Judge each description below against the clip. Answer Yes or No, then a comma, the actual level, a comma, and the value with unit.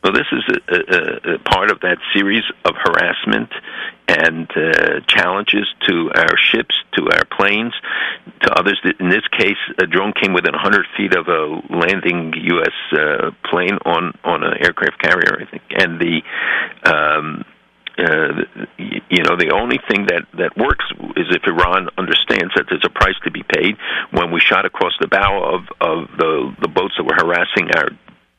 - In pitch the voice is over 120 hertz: No, low, 115 Hz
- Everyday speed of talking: Yes, average, 175 wpm